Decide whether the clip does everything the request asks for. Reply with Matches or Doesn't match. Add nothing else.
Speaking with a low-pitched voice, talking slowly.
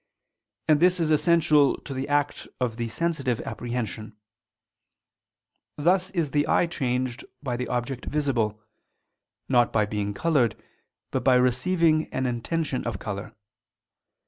Matches